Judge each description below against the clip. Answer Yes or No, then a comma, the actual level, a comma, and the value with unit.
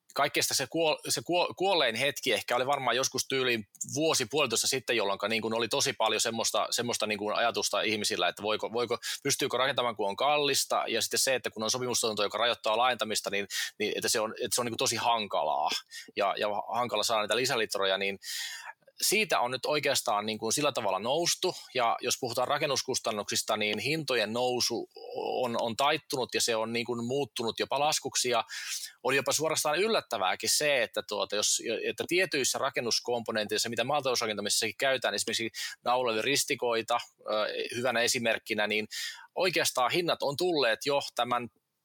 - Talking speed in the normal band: No, fast, 160 wpm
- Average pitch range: Yes, average, 4.7 semitones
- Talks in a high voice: No, low, 120 Hz